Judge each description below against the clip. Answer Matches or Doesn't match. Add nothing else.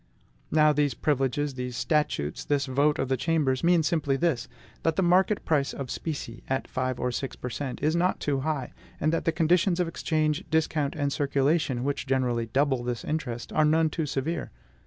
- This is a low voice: Doesn't match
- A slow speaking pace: Doesn't match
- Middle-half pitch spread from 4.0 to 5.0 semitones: Doesn't match